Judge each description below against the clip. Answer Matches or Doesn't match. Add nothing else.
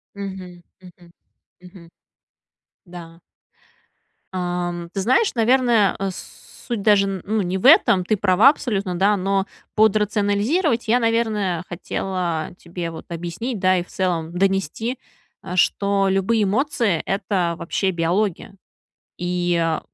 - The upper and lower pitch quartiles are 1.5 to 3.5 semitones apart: Matches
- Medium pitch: Doesn't match